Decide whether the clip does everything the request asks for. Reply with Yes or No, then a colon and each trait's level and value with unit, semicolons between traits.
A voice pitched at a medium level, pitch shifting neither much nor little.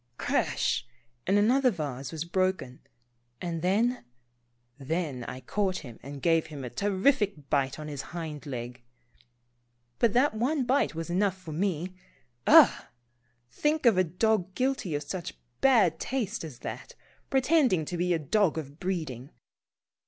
No: medium, 175 Hz; wide, 6.2 semitones